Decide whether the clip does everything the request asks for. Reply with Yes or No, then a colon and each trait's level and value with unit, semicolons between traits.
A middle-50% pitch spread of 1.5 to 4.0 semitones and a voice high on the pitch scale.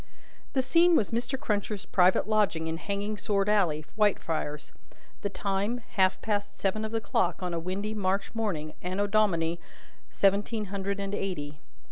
Yes: average, 2.7 semitones; high, 200 Hz